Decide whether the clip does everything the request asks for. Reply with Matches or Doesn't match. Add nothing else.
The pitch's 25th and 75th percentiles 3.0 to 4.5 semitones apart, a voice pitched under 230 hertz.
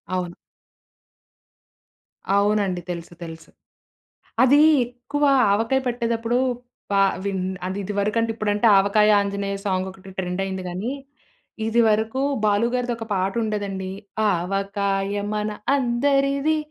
Matches